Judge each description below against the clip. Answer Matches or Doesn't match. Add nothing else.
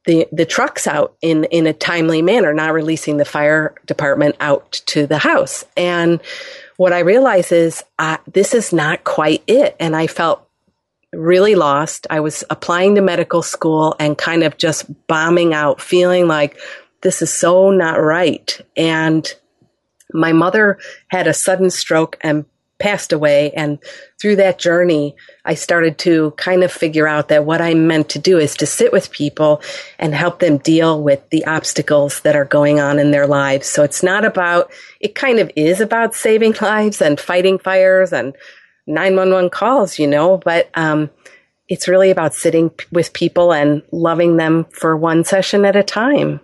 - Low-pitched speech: Doesn't match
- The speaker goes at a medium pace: Matches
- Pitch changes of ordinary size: Matches